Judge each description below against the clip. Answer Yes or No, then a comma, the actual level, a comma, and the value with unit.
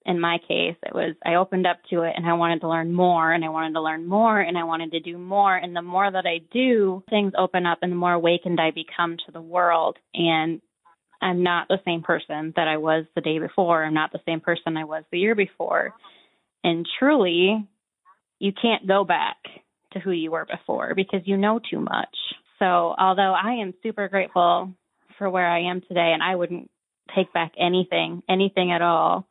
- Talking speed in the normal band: No, fast, 215 wpm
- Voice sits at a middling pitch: Yes, medium, 175 Hz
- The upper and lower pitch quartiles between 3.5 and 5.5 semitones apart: No, narrow, 2.4 semitones